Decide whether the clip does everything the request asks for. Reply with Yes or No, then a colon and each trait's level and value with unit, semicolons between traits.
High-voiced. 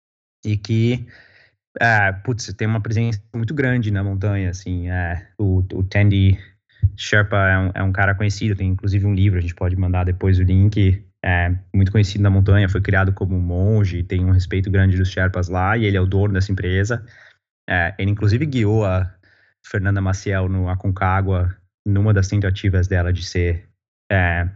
No: very low, 95 Hz